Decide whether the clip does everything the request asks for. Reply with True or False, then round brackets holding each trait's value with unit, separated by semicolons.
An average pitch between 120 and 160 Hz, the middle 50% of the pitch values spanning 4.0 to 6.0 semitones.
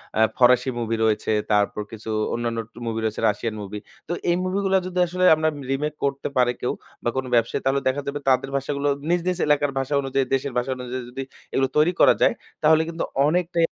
True (135 Hz; 4.6 semitones)